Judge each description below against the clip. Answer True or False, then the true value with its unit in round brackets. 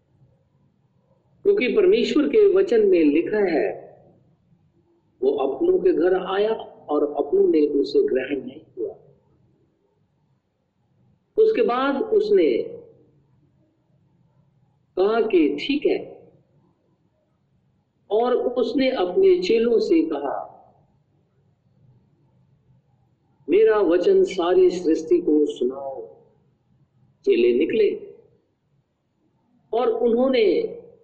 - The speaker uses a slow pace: True (80 wpm)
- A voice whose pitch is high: True (345 Hz)